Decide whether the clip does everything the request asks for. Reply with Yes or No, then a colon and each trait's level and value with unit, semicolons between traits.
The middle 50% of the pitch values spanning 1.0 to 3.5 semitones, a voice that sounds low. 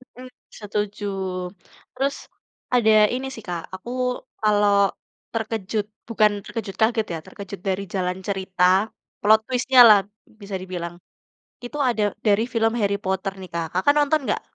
No: average, 3.1 semitones; high, 210 Hz